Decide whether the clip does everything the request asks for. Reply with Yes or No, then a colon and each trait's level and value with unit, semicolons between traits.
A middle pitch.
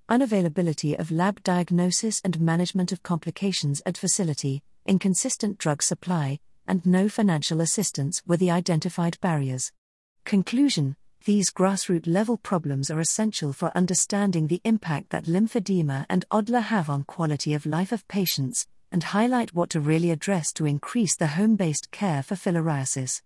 Yes: medium, 180 Hz